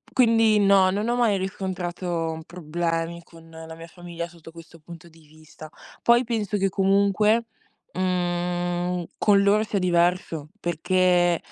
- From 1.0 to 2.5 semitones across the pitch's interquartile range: No, average, 2.9 semitones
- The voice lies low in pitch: No, medium, 175 Hz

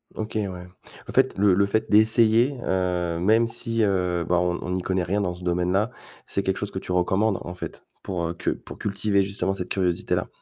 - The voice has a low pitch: Yes, very low, 95 Hz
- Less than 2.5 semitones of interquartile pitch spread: No, average, 2.8 semitones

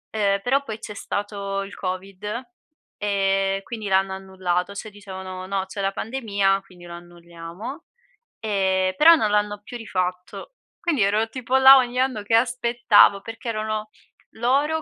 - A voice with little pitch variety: No, average, 3.1 semitones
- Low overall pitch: No, high, 205 Hz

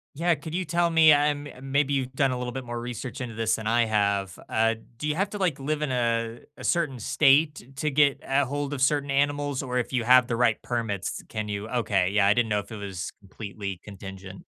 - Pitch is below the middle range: Yes, low, 125 Hz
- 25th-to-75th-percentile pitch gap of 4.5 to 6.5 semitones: Yes, average, 4.8 semitones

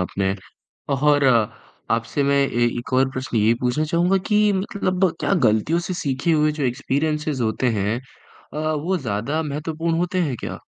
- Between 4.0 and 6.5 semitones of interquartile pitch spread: Yes, average, 4.8 semitones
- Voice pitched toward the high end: No, medium, 145 Hz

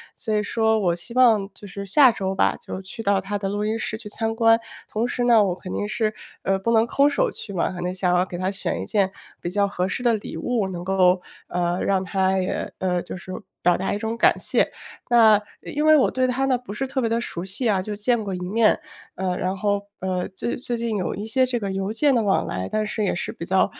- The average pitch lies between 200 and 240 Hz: Yes, high, 205 Hz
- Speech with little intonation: No, average, 3.4 semitones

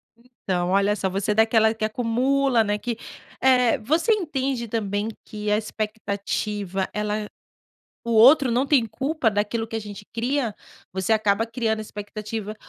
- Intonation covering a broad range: No, average, 2.7 semitones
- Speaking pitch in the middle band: No, high, 220 Hz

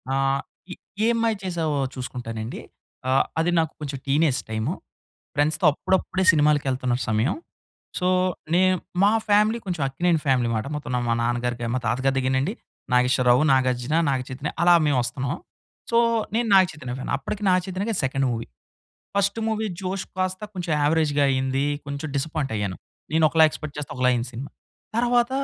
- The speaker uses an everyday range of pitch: No, wide, 6.1 semitones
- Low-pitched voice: No, medium, 145 Hz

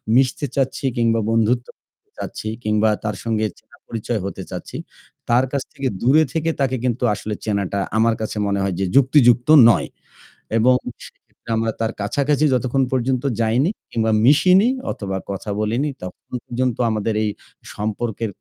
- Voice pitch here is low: Yes, low, 115 Hz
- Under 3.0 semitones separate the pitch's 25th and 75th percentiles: No, average, 3.3 semitones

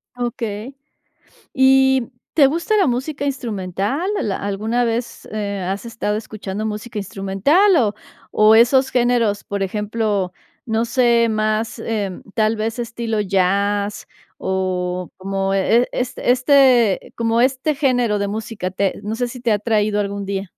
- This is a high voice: Yes, high, 220 Hz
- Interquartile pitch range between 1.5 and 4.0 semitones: Yes, average, 3.4 semitones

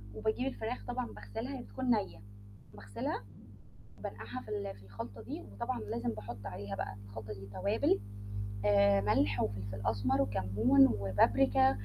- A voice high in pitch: No, low, 105 Hz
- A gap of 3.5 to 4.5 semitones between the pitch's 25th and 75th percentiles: Yes, average, 4.1 semitones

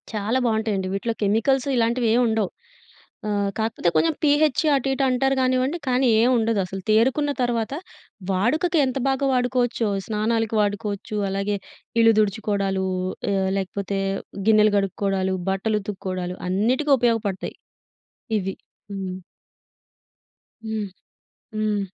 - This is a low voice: No, high, 220 Hz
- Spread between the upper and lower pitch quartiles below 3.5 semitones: No, average, 3.9 semitones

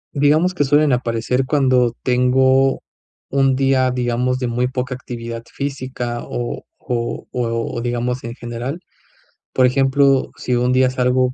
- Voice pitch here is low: Yes, low, 125 Hz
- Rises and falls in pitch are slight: Yes, narrow, 1.7 semitones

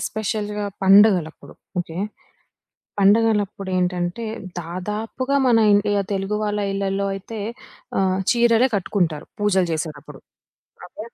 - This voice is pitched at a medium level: No, high, 200 Hz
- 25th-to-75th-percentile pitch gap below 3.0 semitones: Yes, narrow, 2.6 semitones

